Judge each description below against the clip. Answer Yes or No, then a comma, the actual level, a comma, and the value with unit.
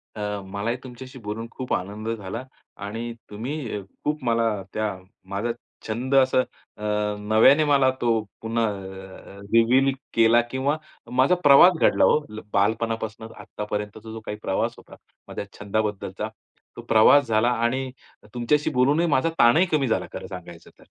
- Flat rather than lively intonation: No, average, 3.7 semitones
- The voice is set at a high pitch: No, low, 115 Hz